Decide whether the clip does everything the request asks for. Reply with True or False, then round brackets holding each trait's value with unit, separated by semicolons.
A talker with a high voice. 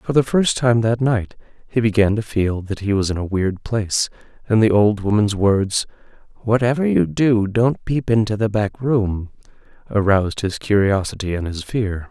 False (105 Hz)